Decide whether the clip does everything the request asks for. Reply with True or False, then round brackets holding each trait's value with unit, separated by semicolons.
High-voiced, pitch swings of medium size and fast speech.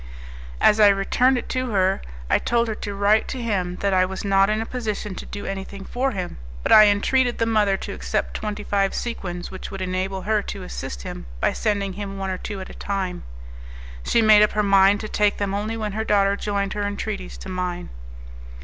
False (200 Hz; 1.9 semitones; 220 wpm)